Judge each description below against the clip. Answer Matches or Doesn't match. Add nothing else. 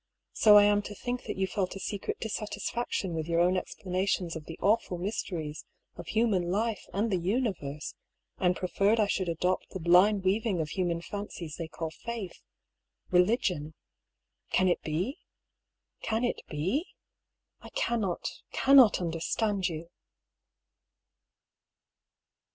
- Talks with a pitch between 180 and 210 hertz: Matches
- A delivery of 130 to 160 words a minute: Matches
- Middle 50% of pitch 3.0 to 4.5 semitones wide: Matches